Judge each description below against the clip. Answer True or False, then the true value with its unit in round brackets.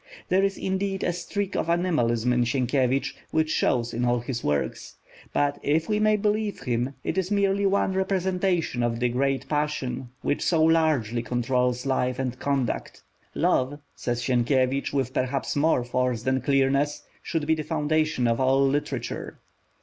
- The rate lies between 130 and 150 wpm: False (160 wpm)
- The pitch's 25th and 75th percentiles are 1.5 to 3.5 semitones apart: False (4.8 semitones)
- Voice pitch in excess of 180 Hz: False (140 Hz)